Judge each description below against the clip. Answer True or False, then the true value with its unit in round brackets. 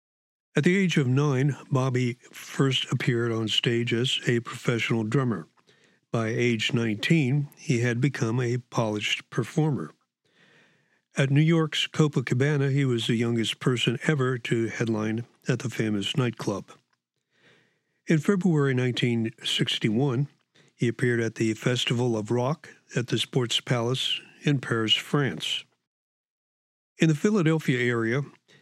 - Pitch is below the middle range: True (125 Hz)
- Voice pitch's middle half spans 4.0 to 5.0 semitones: False (3.5 semitones)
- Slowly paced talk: True (125 wpm)